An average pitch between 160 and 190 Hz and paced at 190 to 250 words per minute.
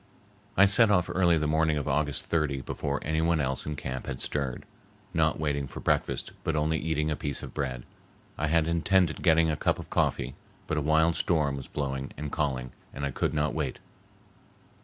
No: very low, 75 Hz; average, 200 wpm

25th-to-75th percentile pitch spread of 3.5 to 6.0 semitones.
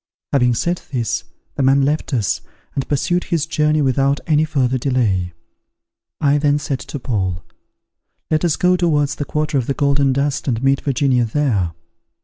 No: average, 3.0 semitones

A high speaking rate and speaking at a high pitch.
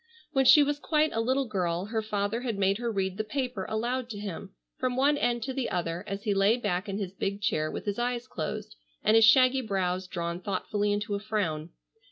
Yes: fast, 225 wpm; high, 210 Hz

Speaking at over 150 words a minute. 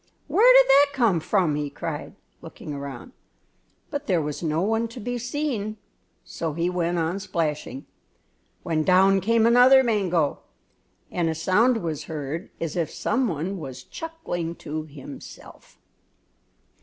No: average, 145 wpm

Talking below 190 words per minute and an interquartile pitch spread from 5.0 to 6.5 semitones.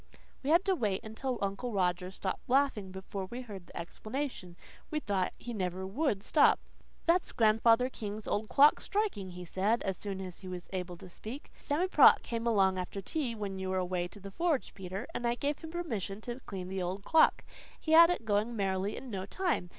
No: fast, 205 wpm; wide, 5.4 semitones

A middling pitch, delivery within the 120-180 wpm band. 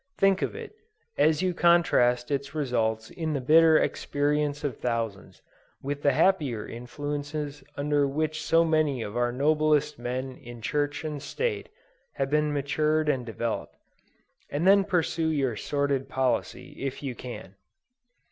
Yes: medium, 145 Hz; average, 145 wpm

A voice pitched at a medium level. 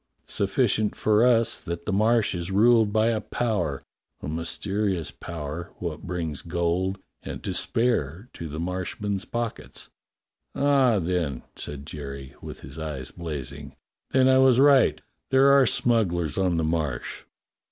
No: very low, 90 Hz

